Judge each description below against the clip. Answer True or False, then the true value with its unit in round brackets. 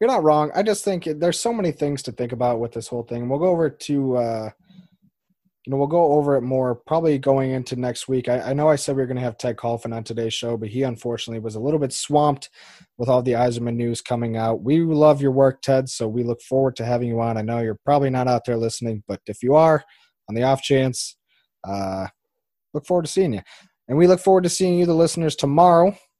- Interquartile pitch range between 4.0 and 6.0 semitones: True (4.6 semitones)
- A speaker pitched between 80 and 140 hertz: True (135 Hz)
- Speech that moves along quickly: True (250 wpm)